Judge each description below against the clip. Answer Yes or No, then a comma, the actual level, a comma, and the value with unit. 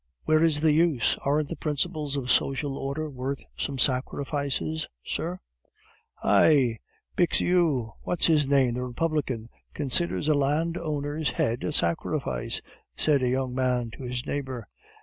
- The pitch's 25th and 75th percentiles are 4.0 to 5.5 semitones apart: No, average, 3.4 semitones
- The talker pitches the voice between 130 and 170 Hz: Yes, medium, 140 Hz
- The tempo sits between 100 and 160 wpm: Yes, slow, 135 wpm